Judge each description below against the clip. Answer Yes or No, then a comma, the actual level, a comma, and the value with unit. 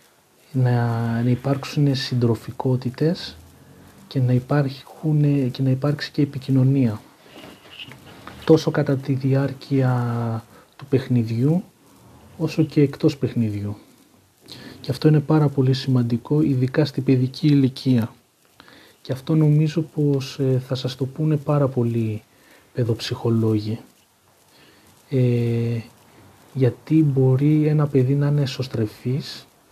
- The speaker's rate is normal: No, slow, 100 wpm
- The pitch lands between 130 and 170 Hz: Yes, low, 135 Hz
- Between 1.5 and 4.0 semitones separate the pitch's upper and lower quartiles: Yes, average, 3.2 semitones